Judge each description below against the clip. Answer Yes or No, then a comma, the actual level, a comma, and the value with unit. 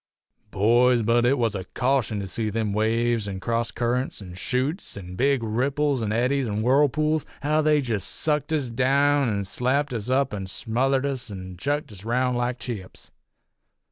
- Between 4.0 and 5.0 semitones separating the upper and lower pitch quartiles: Yes, average, 4.3 semitones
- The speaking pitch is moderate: No, low, 120 Hz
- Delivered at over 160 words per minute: Yes, average, 175 wpm